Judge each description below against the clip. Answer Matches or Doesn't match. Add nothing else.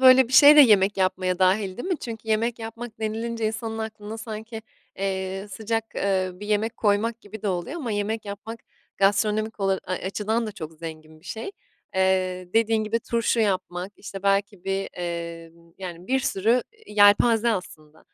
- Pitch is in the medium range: Doesn't match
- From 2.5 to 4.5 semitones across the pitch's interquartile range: Matches